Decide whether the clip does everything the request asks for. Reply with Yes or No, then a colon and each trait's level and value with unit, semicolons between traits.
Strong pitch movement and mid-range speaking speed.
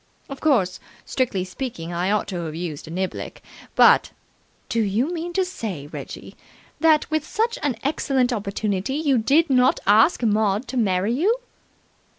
Yes: wide, 7.0 semitones; average, 165 wpm